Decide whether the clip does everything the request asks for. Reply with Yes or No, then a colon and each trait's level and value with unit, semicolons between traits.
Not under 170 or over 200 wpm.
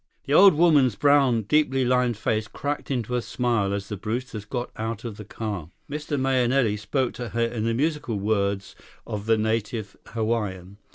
Yes: average, 175 wpm